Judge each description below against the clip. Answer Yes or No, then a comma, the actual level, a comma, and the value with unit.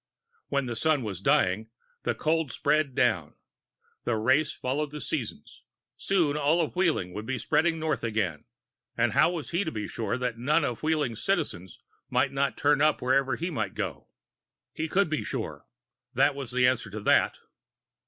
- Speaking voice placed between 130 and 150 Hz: Yes, low, 135 Hz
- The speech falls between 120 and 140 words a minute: No, average, 175 wpm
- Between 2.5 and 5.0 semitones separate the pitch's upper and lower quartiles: No, wide, 5.4 semitones